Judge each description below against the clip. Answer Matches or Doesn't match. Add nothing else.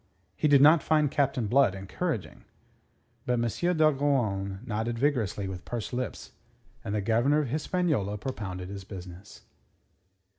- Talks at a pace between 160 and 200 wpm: Doesn't match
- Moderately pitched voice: Doesn't match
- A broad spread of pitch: Matches